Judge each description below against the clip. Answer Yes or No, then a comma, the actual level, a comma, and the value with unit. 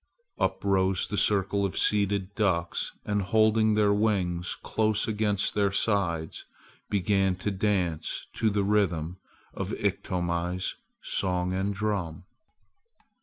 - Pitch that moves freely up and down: No, narrow, 2.5 semitones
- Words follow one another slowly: Yes, slow, 120 wpm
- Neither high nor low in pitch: No, low, 100 Hz